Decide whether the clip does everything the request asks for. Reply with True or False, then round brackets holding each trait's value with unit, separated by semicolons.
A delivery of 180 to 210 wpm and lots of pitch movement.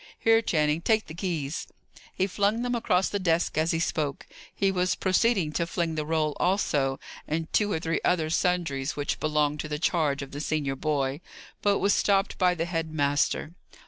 False (190 wpm; 3.7 semitones)